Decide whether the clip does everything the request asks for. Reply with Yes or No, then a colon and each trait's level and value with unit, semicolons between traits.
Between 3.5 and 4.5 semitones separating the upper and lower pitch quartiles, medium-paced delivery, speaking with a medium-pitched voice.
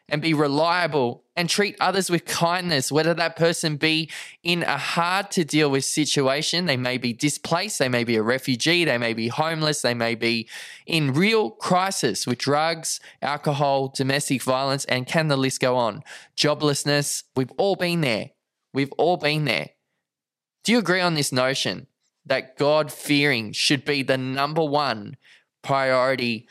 Yes: average, 3.9 semitones; average, 165 wpm; medium, 145 Hz